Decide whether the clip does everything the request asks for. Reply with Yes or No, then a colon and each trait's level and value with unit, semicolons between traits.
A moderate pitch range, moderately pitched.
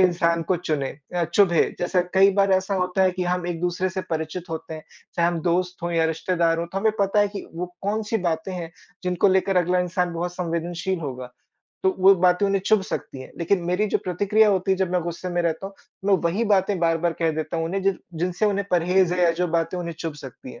No: narrow, 2.2 semitones; medium, 180 Hz